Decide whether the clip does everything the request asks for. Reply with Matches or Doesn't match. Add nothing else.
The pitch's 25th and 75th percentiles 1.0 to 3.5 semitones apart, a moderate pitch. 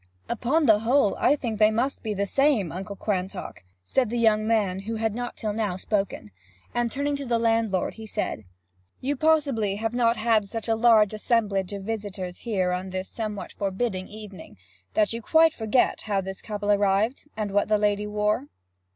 Doesn't match